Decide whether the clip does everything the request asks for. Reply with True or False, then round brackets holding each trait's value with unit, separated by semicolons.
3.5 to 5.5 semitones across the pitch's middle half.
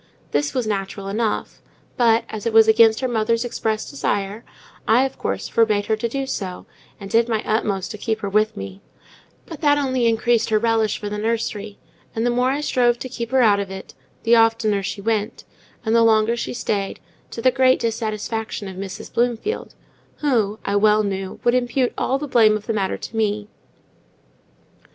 False (2.4 semitones)